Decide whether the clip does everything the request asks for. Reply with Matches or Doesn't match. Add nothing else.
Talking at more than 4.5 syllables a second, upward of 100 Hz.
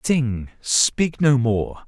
Doesn't match